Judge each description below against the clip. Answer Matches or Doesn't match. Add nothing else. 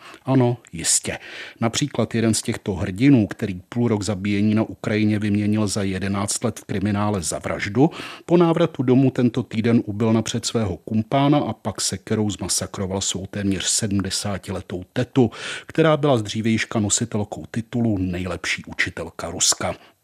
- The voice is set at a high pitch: Doesn't match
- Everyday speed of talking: Matches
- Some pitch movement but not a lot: Matches